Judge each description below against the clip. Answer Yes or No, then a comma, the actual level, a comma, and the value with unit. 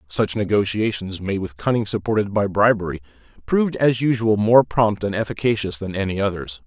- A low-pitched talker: Yes, low, 105 Hz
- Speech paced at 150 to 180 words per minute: Yes, average, 160 wpm